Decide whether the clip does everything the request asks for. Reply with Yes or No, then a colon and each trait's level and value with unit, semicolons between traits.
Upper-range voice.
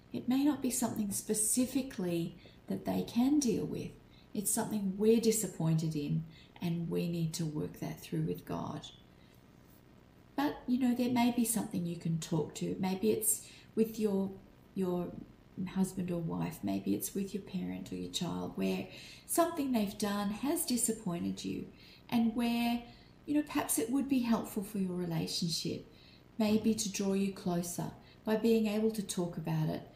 Yes: high, 195 Hz